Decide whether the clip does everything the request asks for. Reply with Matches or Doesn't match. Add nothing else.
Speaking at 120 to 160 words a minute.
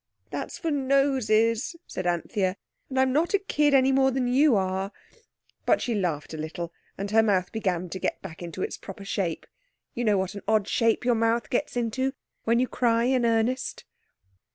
Doesn't match